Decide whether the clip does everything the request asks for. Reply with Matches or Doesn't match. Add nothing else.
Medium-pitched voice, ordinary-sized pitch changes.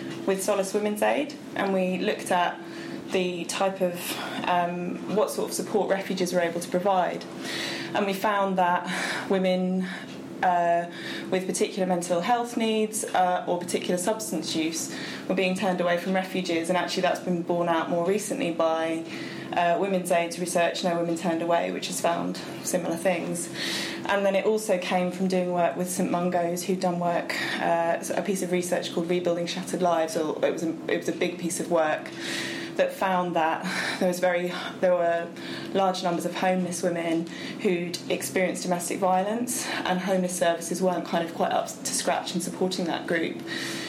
Doesn't match